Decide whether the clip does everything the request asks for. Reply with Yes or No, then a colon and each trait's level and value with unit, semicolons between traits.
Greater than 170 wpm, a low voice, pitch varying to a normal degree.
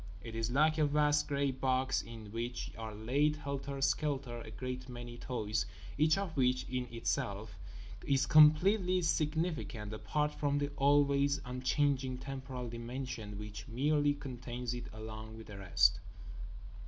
No: average, 140 wpm; low, 130 Hz; average, 4.1 semitones